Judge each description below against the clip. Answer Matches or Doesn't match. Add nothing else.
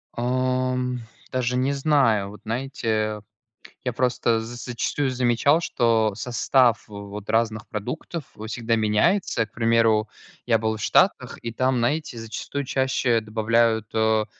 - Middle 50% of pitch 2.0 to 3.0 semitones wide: Matches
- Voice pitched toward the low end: Matches